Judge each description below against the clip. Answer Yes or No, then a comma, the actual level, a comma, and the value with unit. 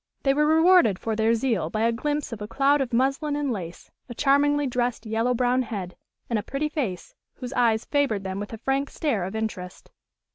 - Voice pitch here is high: Yes, high, 240 Hz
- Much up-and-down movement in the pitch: No, average, 4.4 semitones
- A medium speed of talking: No, fast, 210 wpm